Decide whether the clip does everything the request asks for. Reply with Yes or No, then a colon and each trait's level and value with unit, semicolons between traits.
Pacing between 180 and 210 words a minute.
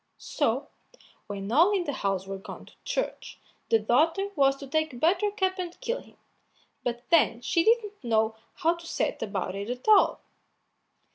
No: average, 165 wpm